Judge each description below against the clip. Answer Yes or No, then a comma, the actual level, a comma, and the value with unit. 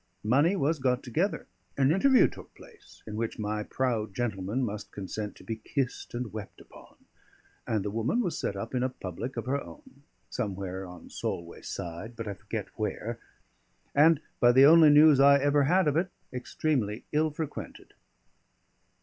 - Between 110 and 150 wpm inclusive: No, average, 170 wpm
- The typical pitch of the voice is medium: No, low, 125 Hz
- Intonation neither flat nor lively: No, wide, 5.7 semitones